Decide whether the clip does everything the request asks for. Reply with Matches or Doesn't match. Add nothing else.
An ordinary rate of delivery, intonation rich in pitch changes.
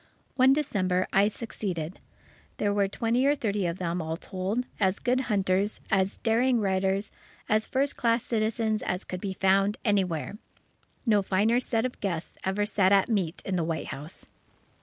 Doesn't match